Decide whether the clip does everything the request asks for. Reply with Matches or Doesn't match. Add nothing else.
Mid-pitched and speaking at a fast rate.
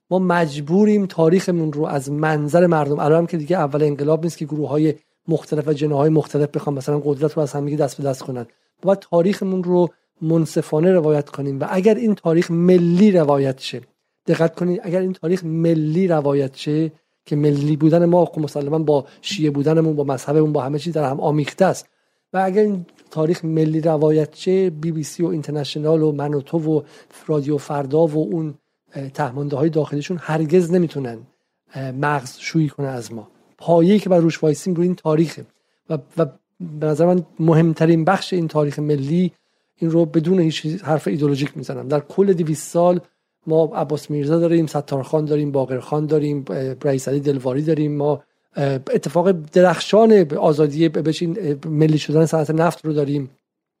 Matches